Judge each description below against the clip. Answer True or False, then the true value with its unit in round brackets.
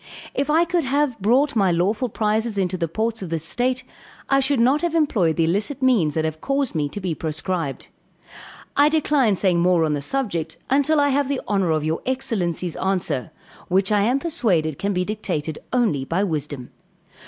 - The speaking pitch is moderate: False (200 Hz)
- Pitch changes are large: True (7.9 semitones)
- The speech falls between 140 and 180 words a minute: False (190 wpm)